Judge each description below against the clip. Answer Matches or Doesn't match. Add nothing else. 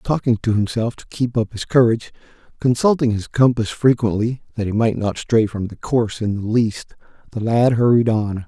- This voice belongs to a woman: Doesn't match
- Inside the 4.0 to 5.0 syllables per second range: Doesn't match